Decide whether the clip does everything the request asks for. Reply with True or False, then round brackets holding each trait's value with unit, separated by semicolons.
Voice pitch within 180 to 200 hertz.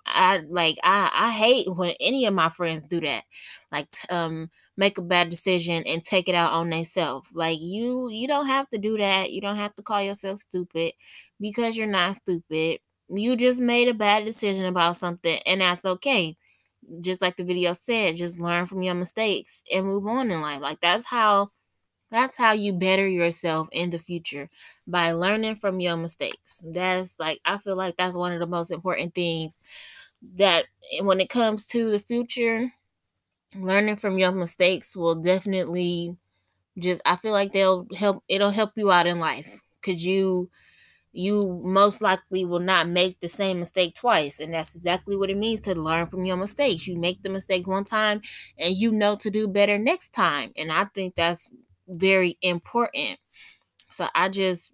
True (185 Hz)